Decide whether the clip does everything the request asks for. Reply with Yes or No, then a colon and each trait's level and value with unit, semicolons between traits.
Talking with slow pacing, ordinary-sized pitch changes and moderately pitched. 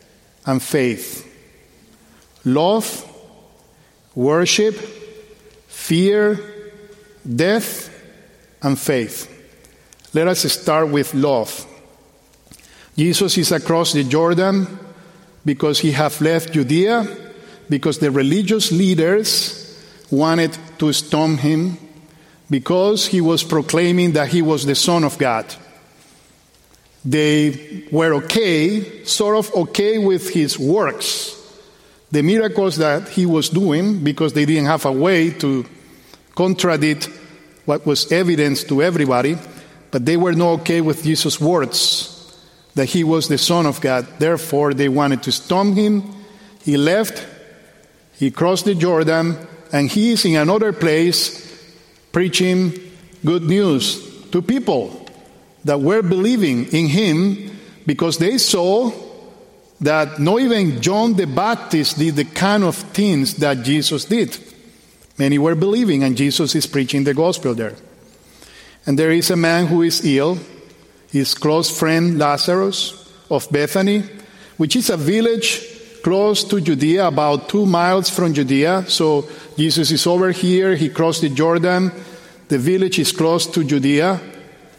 Yes: slow, 130 wpm; average, 4.0 semitones; medium, 165 Hz